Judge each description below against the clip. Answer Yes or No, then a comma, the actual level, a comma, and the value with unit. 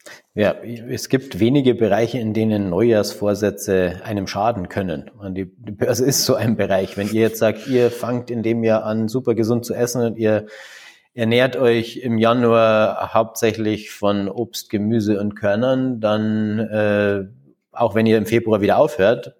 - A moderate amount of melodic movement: No, narrow, 2.3 semitones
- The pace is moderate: Yes, average, 165 wpm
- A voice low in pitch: Yes, low, 110 Hz